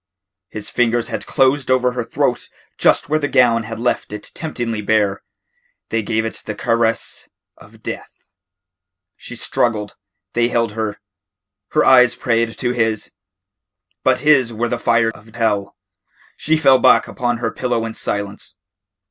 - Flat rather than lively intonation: Yes, narrow, 1.8 semitones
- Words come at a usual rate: Yes, average, 150 wpm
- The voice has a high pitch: No, low, 115 Hz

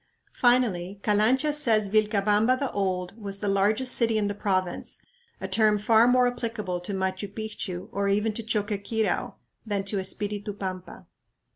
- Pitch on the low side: No, high, 205 Hz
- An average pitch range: No, narrow, 2.2 semitones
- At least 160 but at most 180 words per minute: No, average, 150 wpm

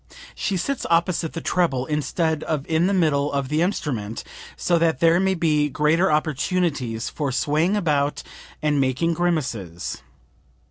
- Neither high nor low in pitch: Yes, medium, 155 Hz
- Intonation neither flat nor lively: Yes, average, 3.4 semitones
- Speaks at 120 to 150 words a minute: Yes, average, 145 wpm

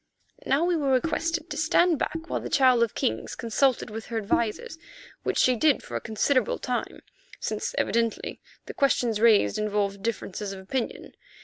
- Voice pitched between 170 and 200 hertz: No, high, 235 Hz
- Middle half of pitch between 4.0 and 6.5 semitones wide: Yes, average, 4.9 semitones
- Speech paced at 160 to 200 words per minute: Yes, average, 170 wpm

